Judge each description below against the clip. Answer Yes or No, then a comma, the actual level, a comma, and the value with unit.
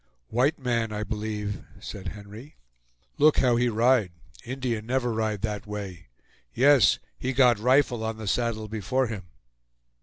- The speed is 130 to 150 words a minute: Yes, average, 145 wpm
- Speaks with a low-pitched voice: Yes, low, 115 Hz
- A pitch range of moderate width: Yes, average, 3.1 semitones